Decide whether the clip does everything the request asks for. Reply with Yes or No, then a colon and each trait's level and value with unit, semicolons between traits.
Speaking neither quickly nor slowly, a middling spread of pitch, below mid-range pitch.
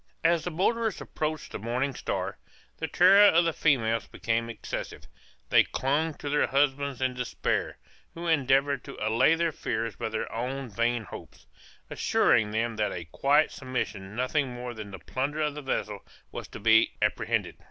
Yes: average, 170 wpm; average, 5.0 semitones; low, 130 Hz